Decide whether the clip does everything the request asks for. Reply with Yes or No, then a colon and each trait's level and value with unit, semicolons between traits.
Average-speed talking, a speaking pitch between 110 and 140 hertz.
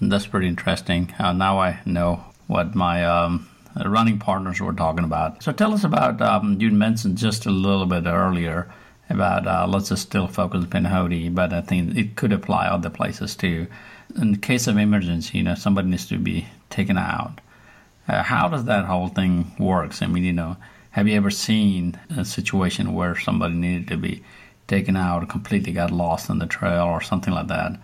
No: average, 195 wpm; very low, 95 Hz